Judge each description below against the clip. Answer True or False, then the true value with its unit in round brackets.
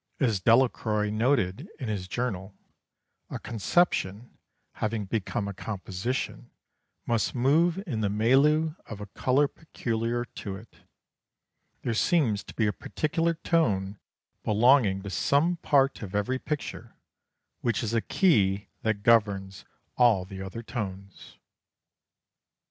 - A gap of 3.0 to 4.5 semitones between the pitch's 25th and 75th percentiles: False (5.0 semitones)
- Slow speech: True (125 wpm)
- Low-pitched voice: True (115 Hz)